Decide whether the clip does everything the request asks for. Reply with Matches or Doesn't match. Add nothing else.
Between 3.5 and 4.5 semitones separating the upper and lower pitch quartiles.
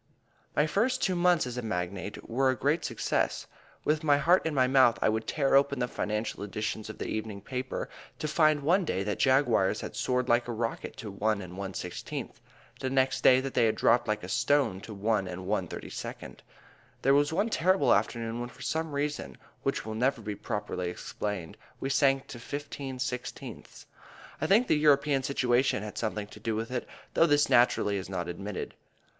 Doesn't match